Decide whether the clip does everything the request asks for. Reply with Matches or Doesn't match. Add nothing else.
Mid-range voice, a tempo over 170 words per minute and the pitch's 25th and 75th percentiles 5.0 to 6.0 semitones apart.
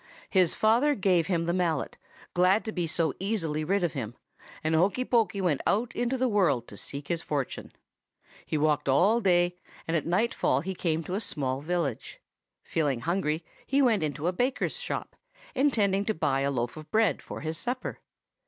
Matches